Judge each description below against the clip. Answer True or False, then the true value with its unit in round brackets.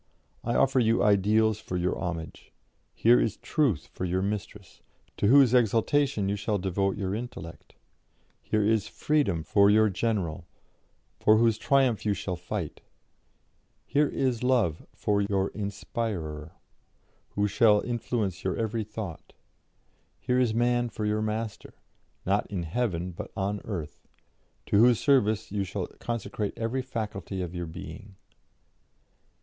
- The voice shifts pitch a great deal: False (3.3 semitones)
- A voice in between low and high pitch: False (105 Hz)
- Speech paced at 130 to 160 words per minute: True (140 wpm)